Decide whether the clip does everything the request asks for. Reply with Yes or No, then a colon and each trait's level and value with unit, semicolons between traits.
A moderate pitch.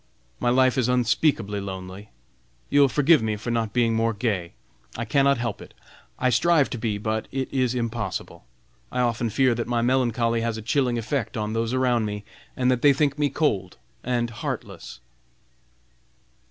No: low, 120 Hz